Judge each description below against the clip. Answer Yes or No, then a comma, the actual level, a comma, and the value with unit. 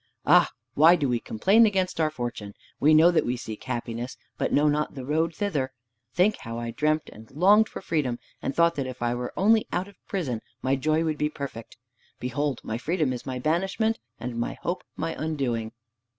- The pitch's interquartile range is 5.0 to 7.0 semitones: Yes, wide, 5.5 semitones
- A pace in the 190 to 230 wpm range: Yes, average, 200 wpm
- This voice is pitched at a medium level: Yes, medium, 150 Hz